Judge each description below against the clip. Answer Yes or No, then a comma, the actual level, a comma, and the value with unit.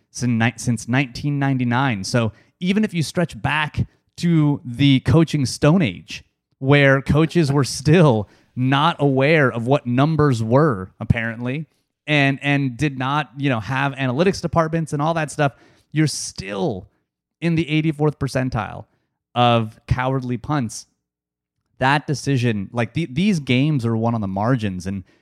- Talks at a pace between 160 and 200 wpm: No, average, 140 wpm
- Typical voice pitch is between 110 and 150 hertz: Yes, low, 135 Hz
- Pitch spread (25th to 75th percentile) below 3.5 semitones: No, average, 4.3 semitones